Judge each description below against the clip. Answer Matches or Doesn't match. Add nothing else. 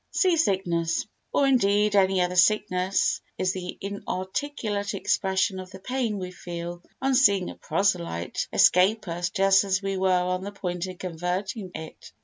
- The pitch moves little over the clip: Matches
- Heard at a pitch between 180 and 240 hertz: Matches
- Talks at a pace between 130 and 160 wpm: Matches